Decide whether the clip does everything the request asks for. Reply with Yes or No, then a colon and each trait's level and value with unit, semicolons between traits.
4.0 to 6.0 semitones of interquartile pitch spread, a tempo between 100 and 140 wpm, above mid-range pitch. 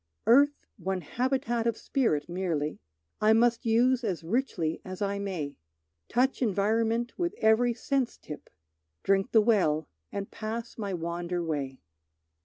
Yes: average, 5.3 semitones; slow, 135 wpm; high, 215 Hz